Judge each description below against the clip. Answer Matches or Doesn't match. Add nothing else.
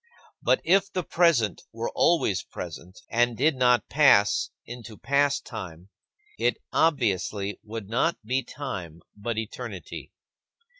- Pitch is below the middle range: Matches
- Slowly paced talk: Matches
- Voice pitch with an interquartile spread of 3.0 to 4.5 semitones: Doesn't match